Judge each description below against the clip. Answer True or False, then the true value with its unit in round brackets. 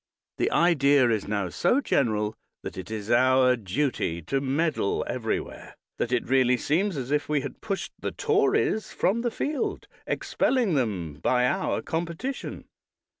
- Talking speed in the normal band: True (150 wpm)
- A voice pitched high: False (135 Hz)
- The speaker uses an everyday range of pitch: False (7.3 semitones)